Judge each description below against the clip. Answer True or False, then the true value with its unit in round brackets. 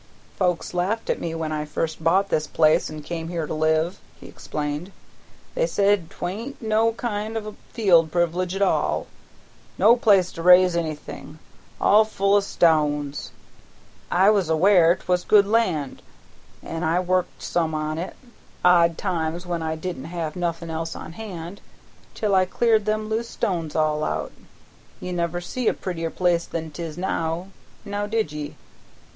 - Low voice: False (175 Hz)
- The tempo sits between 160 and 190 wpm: True (165 wpm)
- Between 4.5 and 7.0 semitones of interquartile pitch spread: False (3.8 semitones)